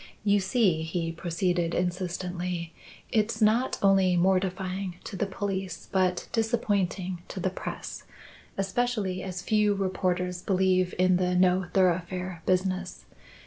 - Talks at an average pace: No, slow, 120 wpm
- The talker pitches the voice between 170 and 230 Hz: Yes, medium, 185 Hz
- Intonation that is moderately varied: No, narrow, 1.4 semitones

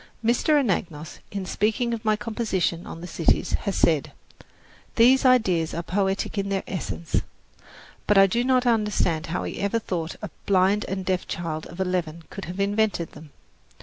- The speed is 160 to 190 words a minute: Yes, average, 170 wpm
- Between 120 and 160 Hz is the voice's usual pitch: No, high, 195 Hz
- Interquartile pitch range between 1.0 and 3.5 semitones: No, average, 4.2 semitones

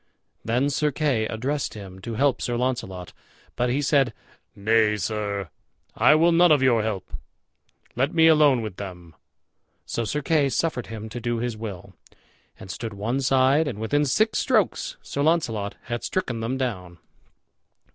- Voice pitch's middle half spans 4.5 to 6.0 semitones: Yes, average, 4.9 semitones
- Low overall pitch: Yes, low, 120 Hz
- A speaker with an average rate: Yes, average, 160 wpm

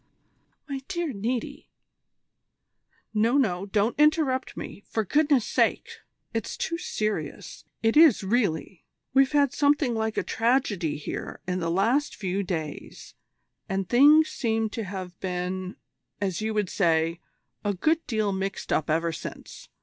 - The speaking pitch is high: Yes, high, 215 Hz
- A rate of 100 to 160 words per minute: Yes, average, 140 wpm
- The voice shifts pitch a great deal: Yes, wide, 6.1 semitones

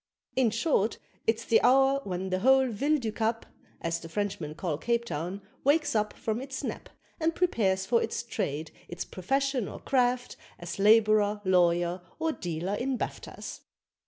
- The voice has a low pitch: No, high, 215 Hz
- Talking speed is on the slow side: No, average, 160 wpm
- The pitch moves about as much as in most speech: No, wide, 5.8 semitones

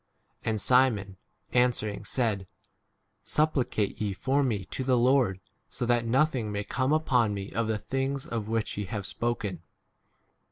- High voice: No, low, 115 Hz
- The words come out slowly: No, average, 150 wpm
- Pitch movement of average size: Yes, average, 4.0 semitones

